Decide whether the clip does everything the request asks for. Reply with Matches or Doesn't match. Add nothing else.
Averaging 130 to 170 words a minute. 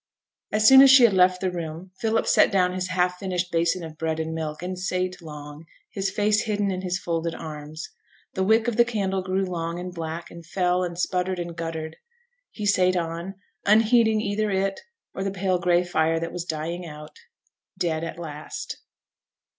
Doesn't match